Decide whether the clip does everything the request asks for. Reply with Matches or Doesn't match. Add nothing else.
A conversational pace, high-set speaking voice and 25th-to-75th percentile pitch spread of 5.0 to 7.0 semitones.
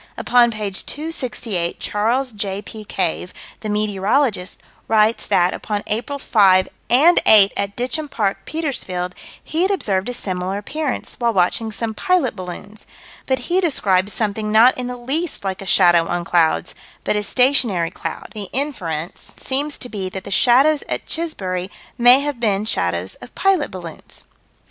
Matches